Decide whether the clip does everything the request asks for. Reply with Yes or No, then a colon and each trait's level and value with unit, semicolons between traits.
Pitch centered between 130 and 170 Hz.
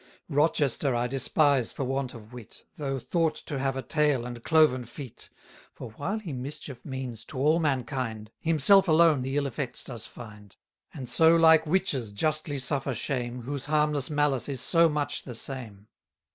Yes: low, 135 Hz